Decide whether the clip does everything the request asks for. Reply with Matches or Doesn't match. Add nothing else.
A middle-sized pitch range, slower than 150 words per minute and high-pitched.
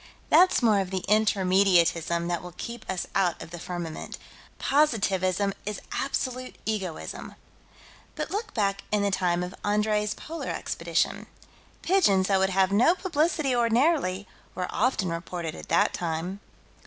Matches